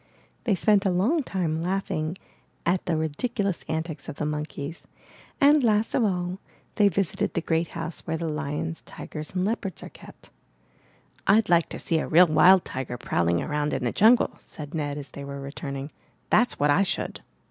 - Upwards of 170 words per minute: Yes, average, 180 wpm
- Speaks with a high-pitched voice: No, medium, 165 Hz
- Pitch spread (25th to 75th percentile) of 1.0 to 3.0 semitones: No, average, 4.6 semitones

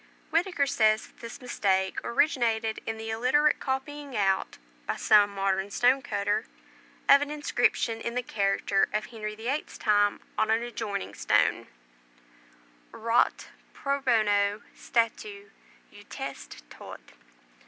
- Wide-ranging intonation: No, average, 3.7 semitones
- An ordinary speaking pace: No, slow, 125 wpm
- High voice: Yes, high, 225 Hz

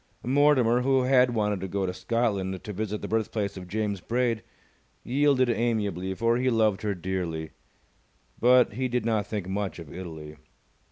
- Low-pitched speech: Yes, low, 110 Hz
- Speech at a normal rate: Yes, average, 165 wpm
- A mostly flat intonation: No, average, 4.4 semitones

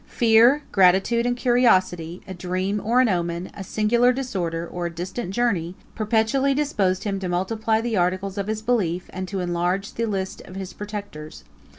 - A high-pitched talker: Yes, high, 195 Hz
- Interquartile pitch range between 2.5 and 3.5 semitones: No, average, 4.2 semitones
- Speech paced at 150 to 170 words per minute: No, average, 180 wpm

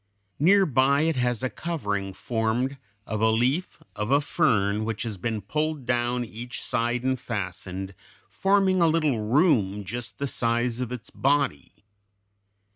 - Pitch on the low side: Yes, low, 120 Hz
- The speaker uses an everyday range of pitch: Yes, average, 4.7 semitones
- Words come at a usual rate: Yes, average, 150 wpm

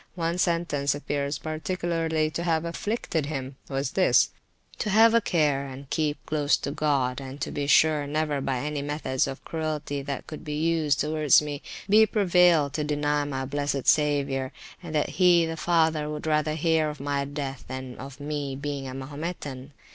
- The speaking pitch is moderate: Yes, medium, 150 Hz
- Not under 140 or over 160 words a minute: No, average, 180 wpm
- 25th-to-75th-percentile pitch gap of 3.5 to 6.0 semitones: No, narrow, 2.4 semitones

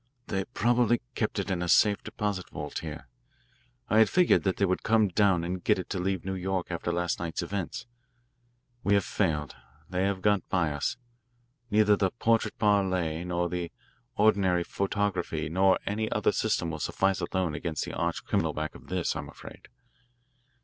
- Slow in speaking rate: No, average, 175 wpm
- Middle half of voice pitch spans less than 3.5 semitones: Yes, average, 2.8 semitones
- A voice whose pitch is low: Yes, very low, 95 Hz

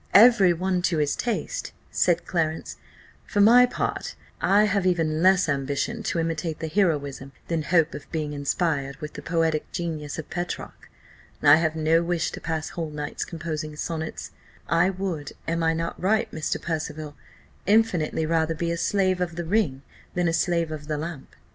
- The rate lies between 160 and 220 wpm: Yes, average, 175 wpm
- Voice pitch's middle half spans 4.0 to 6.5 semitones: No, average, 2.7 semitones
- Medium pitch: Yes, medium, 165 Hz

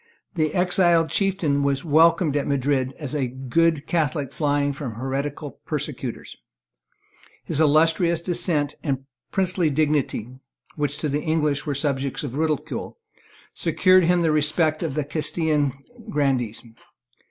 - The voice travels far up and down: No, average, 2.7 semitones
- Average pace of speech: No, slow, 130 wpm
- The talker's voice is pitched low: No, medium, 150 Hz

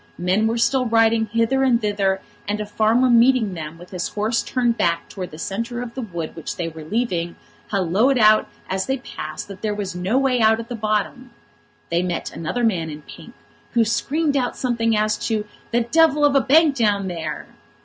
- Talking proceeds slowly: No, average, 200 wpm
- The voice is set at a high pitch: Yes, high, 220 Hz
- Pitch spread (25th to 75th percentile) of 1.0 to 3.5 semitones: No, average, 4.4 semitones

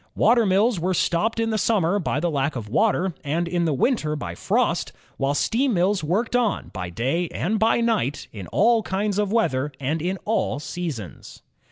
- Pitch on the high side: No, medium, 180 Hz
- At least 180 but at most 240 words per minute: Yes, average, 190 wpm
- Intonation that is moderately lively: No, wide, 6.8 semitones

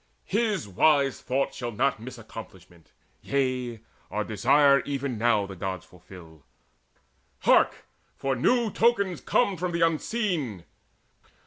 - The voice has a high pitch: No, low, 130 Hz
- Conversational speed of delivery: No, slow, 120 wpm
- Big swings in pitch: Yes, wide, 7.7 semitones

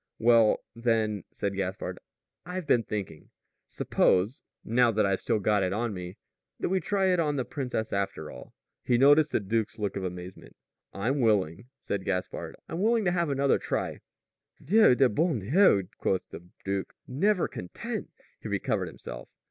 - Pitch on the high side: No, low, 115 Hz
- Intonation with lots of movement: Yes, wide, 6.6 semitones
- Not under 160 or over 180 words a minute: Yes, average, 170 wpm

